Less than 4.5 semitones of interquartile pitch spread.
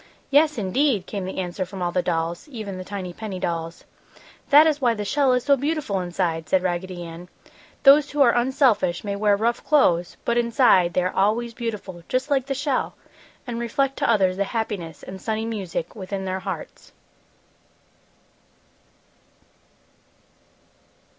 No: wide, 5.5 semitones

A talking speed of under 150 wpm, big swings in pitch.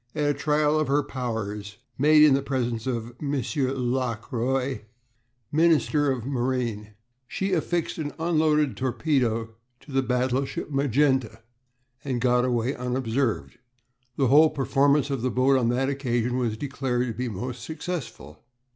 No: average, 140 wpm; average, 3.1 semitones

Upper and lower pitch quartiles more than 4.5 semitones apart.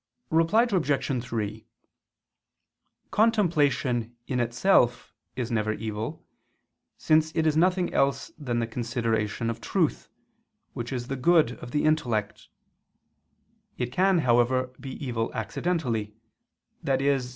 Yes: average, 5.2 semitones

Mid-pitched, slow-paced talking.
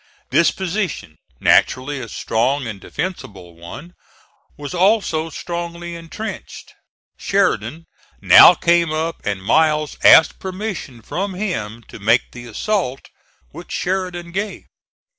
Yes: medium, 165 Hz; slow, 115 wpm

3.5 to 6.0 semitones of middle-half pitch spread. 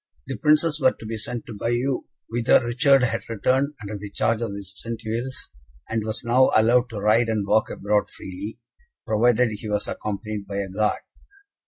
No: narrow, 2.6 semitones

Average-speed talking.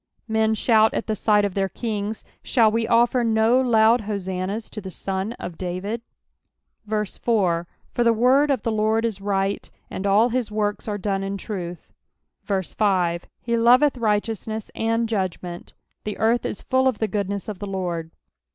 Yes: average, 170 wpm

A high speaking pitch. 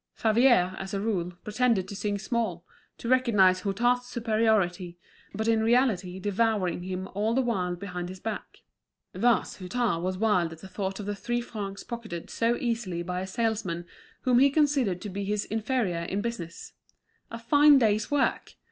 Yes: high, 210 Hz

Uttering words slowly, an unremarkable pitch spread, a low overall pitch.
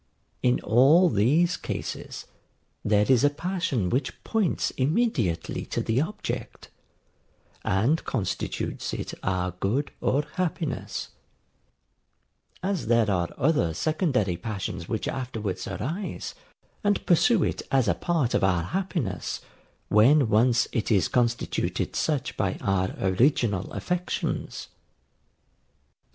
No: slow, 110 wpm; wide, 8.1 semitones; low, 125 Hz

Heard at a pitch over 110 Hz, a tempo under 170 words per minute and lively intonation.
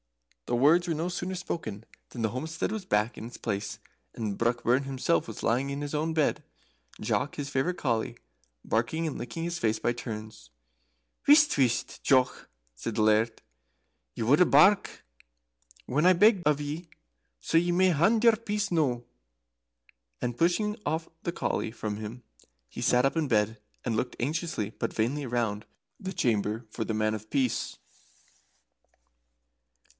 Yes: low, 135 Hz; average, 160 wpm; wide, 6.8 semitones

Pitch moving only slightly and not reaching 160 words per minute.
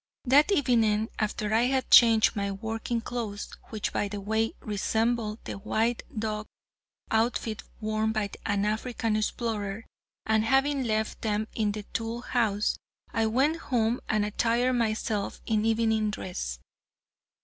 Yes: narrow, 1.8 semitones; average, 140 wpm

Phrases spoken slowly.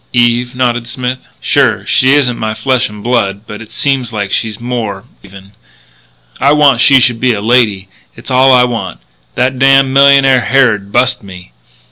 No: average, 170 wpm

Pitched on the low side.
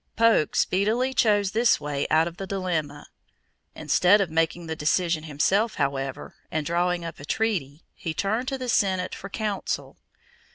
No: medium, 180 Hz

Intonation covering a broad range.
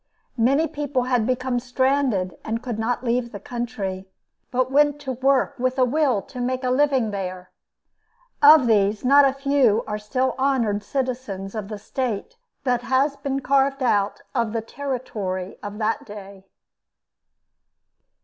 No: average, 4.2 semitones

